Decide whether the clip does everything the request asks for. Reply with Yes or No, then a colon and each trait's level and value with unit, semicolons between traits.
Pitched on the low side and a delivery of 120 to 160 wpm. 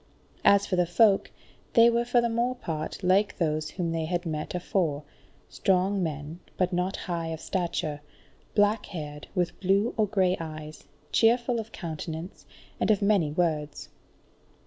No: medium, 180 Hz; average, 155 wpm